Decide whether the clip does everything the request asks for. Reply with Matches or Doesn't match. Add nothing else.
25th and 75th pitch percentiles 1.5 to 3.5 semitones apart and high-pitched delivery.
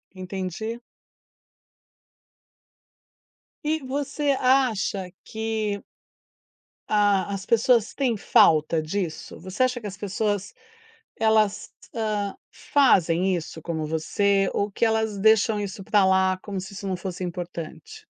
Matches